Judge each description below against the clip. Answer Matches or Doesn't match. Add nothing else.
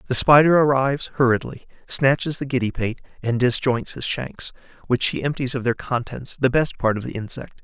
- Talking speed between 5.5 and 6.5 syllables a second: Doesn't match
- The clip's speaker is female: Doesn't match